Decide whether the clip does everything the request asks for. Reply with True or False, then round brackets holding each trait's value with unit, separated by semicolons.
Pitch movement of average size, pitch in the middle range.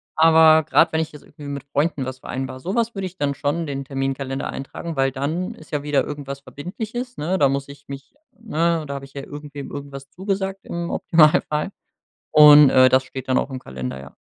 True (3.5 semitones; 145 Hz)